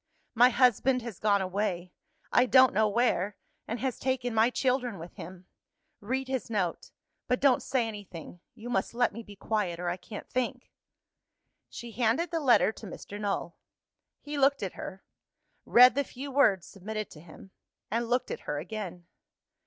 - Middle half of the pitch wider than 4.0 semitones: Yes, average, 4.5 semitones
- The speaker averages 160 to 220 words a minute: Yes, average, 170 wpm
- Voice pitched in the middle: No, high, 225 Hz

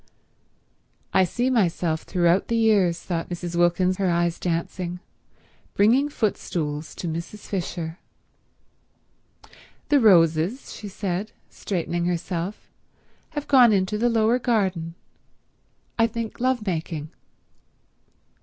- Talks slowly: Yes, slow, 105 wpm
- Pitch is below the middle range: No, medium, 185 Hz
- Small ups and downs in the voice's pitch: No, average, 4.5 semitones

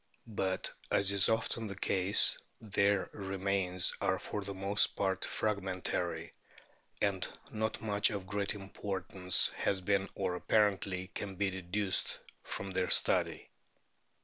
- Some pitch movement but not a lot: No, narrow, 1.5 semitones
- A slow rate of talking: Yes, slow, 130 wpm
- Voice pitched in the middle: No, low, 100 Hz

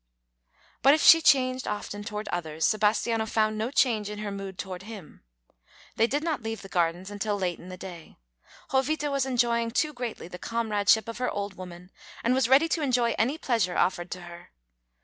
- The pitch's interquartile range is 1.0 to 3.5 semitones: No, average, 4.8 semitones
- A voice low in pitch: No, high, 215 Hz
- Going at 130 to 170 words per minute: No, average, 190 wpm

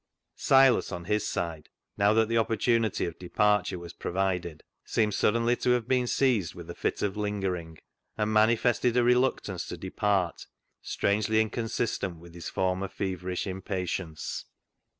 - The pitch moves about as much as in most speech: Yes, average, 3.9 semitones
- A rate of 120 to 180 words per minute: Yes, average, 150 wpm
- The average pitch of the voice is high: No, low, 105 Hz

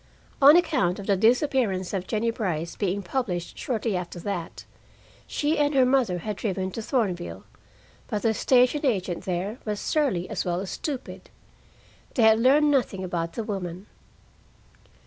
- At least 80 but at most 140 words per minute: No, average, 155 wpm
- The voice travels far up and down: Yes, wide, 5.7 semitones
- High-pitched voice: Yes, high, 210 Hz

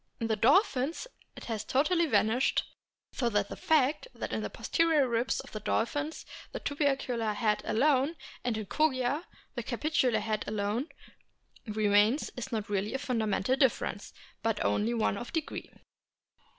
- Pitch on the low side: No, high, 240 Hz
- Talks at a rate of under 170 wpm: Yes, average, 150 wpm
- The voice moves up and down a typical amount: Yes, average, 4.9 semitones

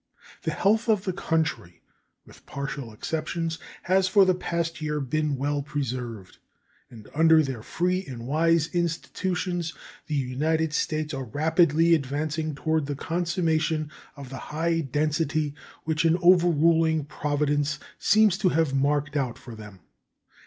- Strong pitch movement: No, average, 2.9 semitones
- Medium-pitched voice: Yes, medium, 155 Hz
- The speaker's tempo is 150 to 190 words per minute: No, average, 140 wpm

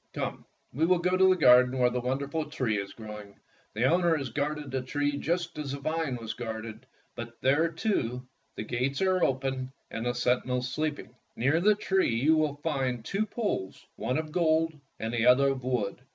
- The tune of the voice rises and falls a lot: No, average, 4.5 semitones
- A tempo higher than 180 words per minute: Yes, average, 200 wpm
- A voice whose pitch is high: No, low, 135 Hz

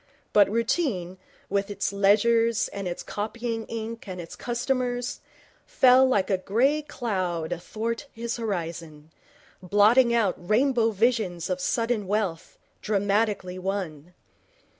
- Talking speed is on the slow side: Yes, slow, 120 wpm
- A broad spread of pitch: No, average, 4.0 semitones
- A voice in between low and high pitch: No, high, 210 Hz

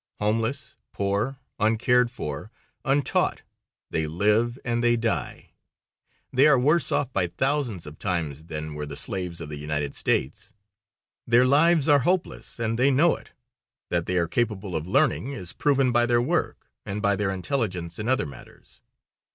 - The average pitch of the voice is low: Yes, low, 110 Hz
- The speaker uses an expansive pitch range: Yes, wide, 7.2 semitones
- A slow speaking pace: No, average, 160 wpm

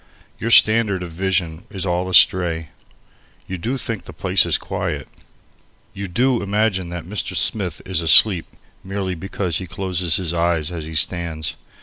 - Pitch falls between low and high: No, very low, 90 Hz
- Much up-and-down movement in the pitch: No, average, 2.9 semitones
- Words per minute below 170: Yes, average, 155 wpm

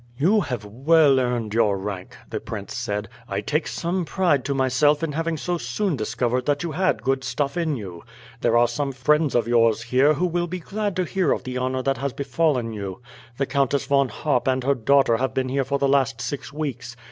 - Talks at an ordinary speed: No, fast, 215 wpm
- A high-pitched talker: No, low, 135 Hz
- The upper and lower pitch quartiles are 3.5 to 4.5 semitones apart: Yes, average, 4.0 semitones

